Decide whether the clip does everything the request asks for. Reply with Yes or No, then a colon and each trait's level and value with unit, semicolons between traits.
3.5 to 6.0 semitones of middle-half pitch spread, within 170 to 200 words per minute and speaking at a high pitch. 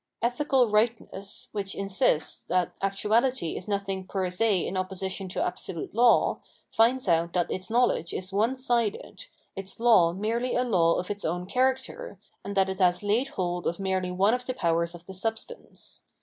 Yes: average, 4.4 semitones; average, 175 wpm; high, 195 Hz